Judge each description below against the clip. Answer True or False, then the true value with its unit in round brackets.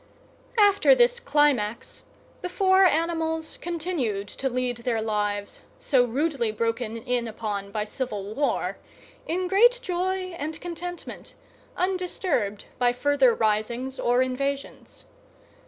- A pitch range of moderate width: False (7.6 semitones)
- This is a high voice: True (275 Hz)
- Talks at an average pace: False (115 wpm)